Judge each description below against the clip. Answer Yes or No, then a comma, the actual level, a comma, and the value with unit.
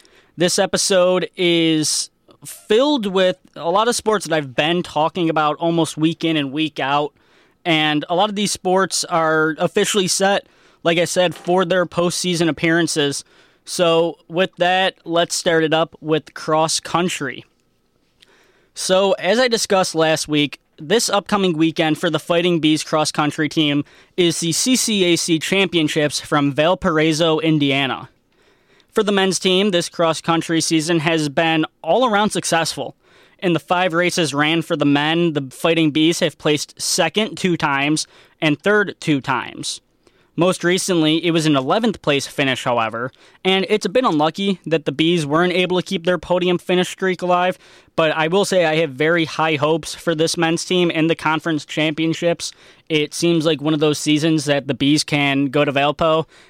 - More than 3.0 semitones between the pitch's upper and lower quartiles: No, average, 2.7 semitones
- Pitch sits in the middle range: Yes, medium, 165 Hz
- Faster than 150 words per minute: Yes, average, 170 wpm